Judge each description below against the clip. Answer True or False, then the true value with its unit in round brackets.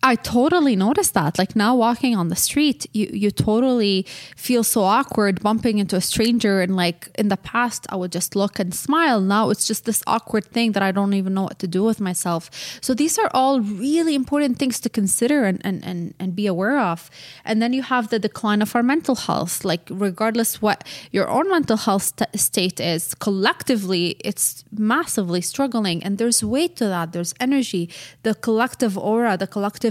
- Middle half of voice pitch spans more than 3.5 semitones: True (4.3 semitones)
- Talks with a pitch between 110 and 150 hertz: False (210 Hz)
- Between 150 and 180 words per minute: False (195 wpm)